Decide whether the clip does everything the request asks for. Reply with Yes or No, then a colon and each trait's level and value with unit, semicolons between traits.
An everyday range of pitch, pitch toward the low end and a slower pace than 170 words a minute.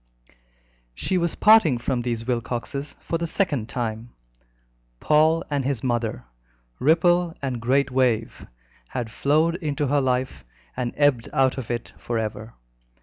Yes: average, 4.2 semitones; low, 130 Hz; average, 140 wpm